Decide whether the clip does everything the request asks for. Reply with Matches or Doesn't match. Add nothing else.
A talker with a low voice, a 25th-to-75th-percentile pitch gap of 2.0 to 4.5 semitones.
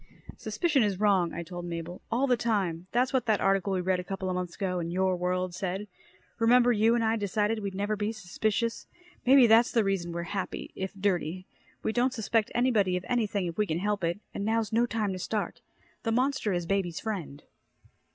Doesn't match